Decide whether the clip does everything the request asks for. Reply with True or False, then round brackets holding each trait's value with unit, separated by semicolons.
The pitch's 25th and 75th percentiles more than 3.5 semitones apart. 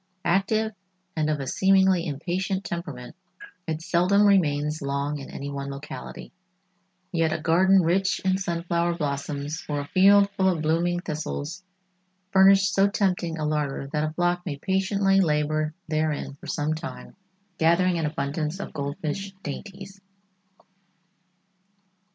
True (4.1 semitones)